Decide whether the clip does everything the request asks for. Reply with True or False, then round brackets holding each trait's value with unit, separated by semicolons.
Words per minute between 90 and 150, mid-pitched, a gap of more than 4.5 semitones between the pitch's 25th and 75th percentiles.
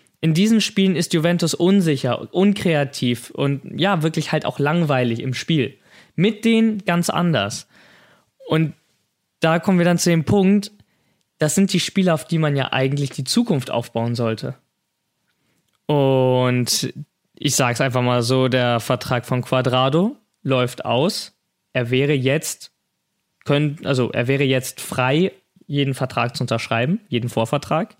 True (145 wpm; 145 Hz; 5.2 semitones)